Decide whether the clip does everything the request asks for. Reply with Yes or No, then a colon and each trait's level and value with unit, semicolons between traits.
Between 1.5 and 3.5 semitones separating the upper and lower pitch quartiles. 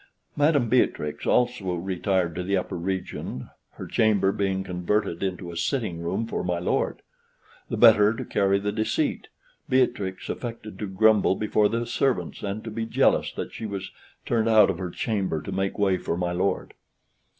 Yes: average, 3.1 semitones